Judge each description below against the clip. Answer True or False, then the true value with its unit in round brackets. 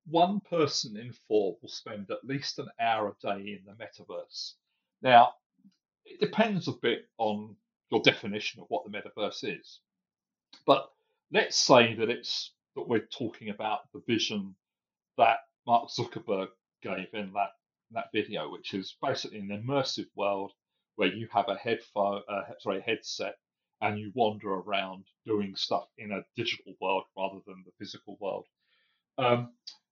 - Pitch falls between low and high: False (115 Hz)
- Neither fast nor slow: True (160 wpm)